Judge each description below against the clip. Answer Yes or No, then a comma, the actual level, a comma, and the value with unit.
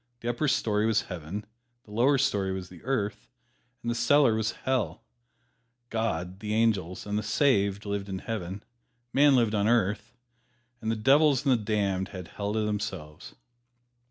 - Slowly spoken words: No, average, 165 wpm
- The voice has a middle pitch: No, low, 105 Hz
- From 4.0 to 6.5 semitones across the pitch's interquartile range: No, average, 3.2 semitones